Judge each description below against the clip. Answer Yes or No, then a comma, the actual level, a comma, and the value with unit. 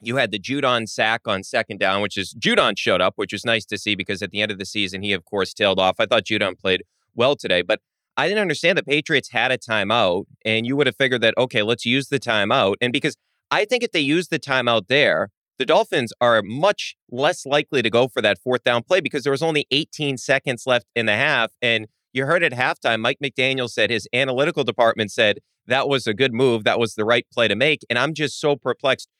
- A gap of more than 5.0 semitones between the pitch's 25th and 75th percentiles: No, average, 4.3 semitones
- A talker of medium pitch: No, low, 120 Hz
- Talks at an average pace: No, fast, 245 wpm